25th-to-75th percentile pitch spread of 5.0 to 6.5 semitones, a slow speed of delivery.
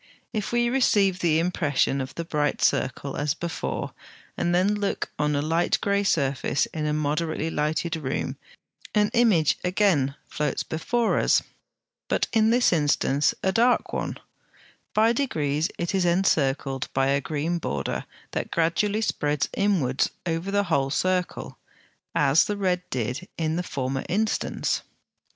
No: wide, 5.4 semitones; average, 145 wpm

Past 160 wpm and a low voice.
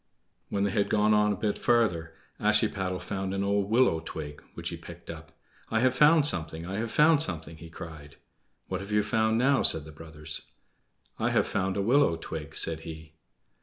Yes: average, 195 wpm; very low, 95 Hz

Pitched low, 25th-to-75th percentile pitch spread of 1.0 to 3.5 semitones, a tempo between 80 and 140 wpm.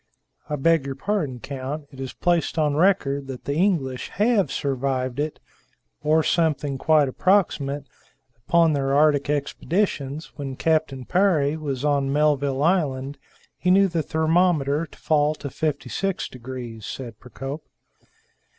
No: medium, 145 Hz; average, 3.1 semitones; slow, 135 wpm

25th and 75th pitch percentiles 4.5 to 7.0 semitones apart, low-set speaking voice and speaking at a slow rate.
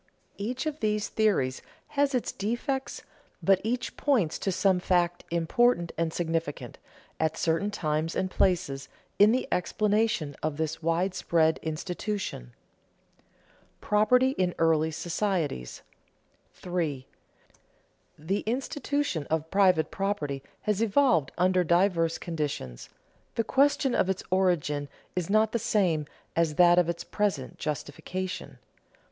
No: average, 4.8 semitones; medium, 180 Hz; slow, 120 wpm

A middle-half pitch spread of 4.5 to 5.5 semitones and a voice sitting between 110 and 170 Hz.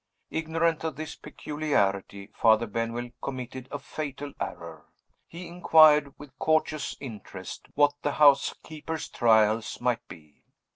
Yes: average, 5.2 semitones; medium, 140 Hz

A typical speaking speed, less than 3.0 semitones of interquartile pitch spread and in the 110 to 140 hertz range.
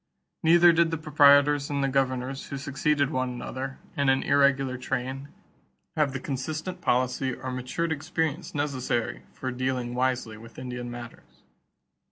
Yes: average, 150 wpm; narrow, 2.4 semitones; low, 135 Hz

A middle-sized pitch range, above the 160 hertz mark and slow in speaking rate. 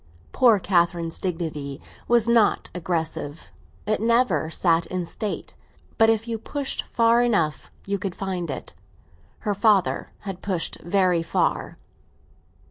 Yes: average, 4.8 semitones; high, 190 Hz; slow, 125 wpm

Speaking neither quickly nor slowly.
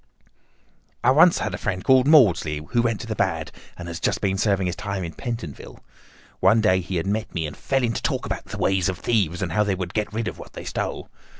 No: fast, 240 wpm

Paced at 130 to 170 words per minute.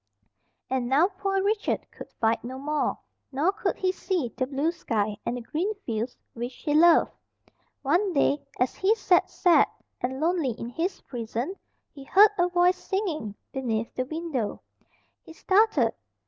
Yes: average, 160 wpm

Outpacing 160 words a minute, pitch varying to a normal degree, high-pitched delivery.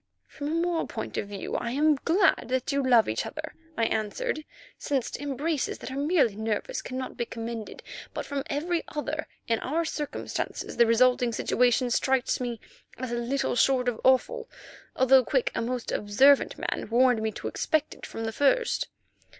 Yes: average, 175 wpm; average, 4.2 semitones; very high, 260 Hz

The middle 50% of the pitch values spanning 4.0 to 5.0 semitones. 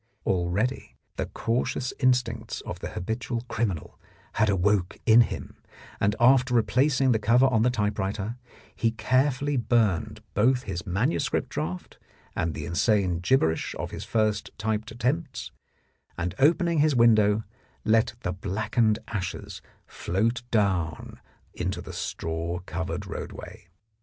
Yes: average, 4.5 semitones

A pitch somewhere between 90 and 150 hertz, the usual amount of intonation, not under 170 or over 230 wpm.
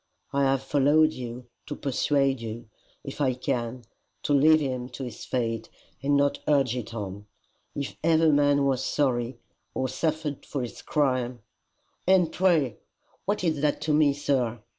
No: low, 135 Hz; average, 3.2 semitones; average, 160 wpm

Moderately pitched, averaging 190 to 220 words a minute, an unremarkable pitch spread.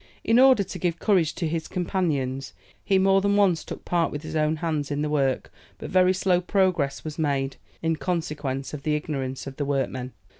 Yes: medium, 155 Hz; average, 200 wpm; average, 4.5 semitones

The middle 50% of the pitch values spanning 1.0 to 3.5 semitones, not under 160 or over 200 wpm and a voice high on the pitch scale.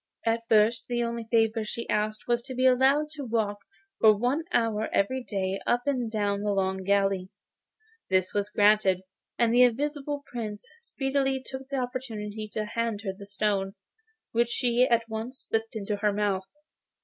Yes: average, 3.2 semitones; average, 170 wpm; high, 225 Hz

